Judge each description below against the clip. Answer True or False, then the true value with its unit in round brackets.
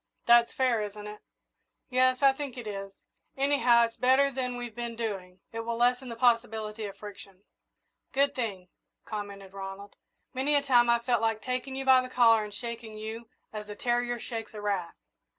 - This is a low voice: False (235 Hz)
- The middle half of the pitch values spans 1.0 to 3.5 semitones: True (3.1 semitones)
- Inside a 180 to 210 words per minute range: True (185 wpm)